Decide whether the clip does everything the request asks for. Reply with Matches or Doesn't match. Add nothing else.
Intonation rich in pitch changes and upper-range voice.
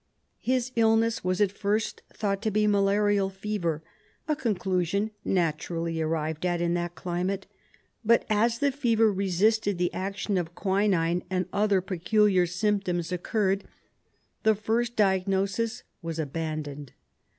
Doesn't match